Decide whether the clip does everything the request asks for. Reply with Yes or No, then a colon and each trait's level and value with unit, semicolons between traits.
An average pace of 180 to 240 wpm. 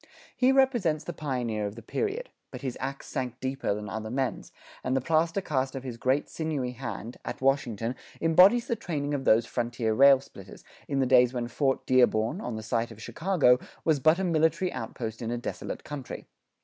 Yes: average, 190 wpm